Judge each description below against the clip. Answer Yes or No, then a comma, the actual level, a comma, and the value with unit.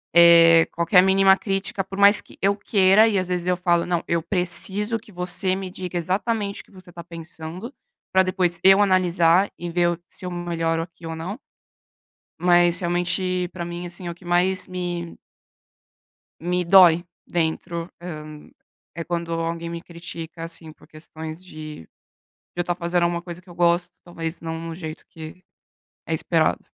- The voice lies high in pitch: No, medium, 175 Hz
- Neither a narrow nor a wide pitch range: No, narrow, 1.7 semitones